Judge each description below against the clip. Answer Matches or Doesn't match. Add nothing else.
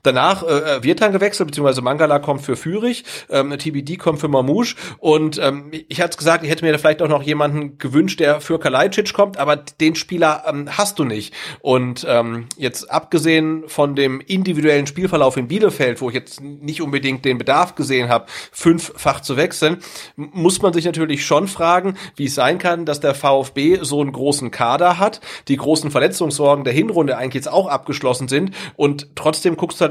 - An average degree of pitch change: Matches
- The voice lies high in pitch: Doesn't match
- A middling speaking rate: Doesn't match